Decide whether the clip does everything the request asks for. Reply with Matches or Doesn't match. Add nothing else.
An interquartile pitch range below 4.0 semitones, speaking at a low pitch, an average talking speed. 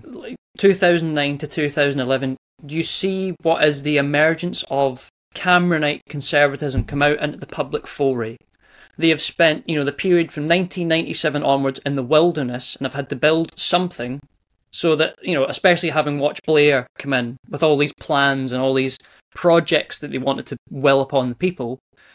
Doesn't match